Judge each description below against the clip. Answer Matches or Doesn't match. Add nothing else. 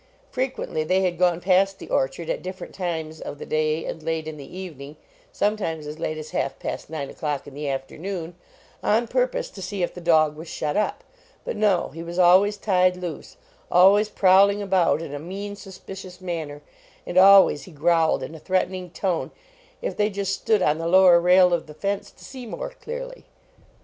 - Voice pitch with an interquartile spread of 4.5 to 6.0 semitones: Doesn't match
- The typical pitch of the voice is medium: Matches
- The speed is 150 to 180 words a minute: Doesn't match